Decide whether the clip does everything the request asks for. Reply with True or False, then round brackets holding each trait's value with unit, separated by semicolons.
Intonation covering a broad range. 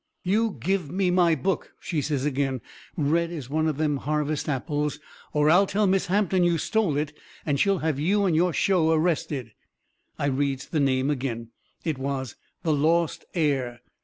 False (4.0 semitones)